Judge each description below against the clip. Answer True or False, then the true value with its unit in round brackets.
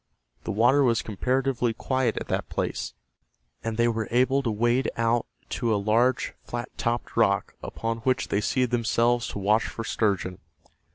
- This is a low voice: True (115 Hz)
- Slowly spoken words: False (165 wpm)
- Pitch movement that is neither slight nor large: False (2.0 semitones)